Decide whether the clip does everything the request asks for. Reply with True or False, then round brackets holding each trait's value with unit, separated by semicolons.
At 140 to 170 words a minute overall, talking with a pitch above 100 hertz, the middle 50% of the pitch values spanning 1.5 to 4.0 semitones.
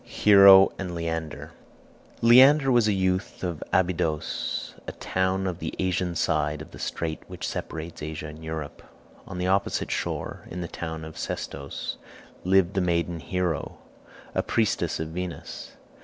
False (150 wpm; 90 Hz; 3.0 semitones)